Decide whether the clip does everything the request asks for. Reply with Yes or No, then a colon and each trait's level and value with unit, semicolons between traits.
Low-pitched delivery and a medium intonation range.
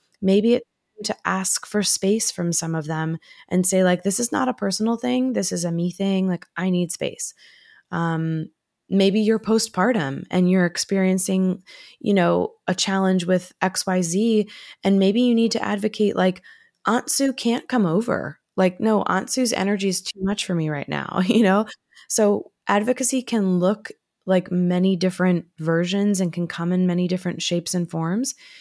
No: high, 190 Hz; average, 3.6 semitones